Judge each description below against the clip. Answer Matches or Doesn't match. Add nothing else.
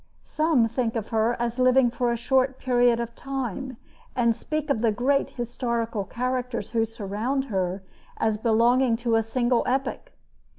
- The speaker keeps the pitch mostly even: Matches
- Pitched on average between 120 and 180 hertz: Doesn't match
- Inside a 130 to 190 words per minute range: Matches